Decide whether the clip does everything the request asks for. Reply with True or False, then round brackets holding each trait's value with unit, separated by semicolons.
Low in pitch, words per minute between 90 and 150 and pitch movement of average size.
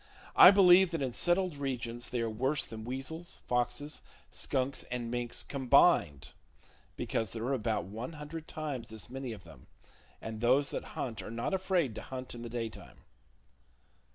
False (125 Hz; 165 wpm; 4.4 semitones)